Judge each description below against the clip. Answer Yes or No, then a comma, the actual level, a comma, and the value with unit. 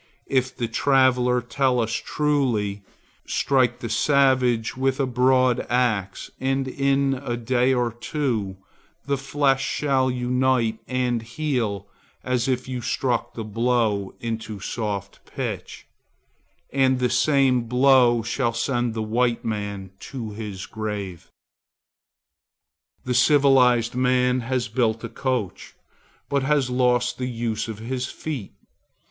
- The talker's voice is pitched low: Yes, low, 125 Hz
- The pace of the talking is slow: Yes, slow, 125 wpm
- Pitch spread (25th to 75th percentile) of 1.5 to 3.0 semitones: Yes, narrow, 2.4 semitones